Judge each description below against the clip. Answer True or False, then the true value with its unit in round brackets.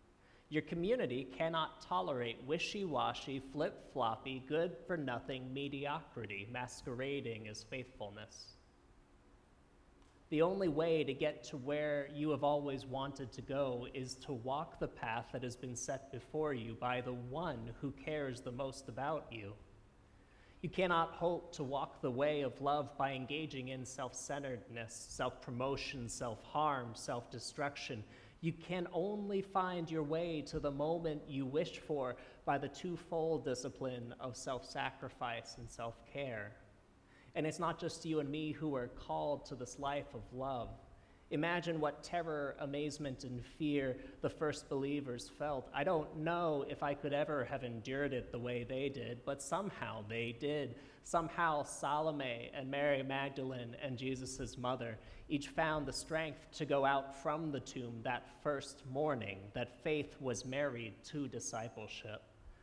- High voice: False (135 Hz)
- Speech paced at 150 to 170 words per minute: True (155 wpm)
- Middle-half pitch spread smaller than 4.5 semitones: True (3.7 semitones)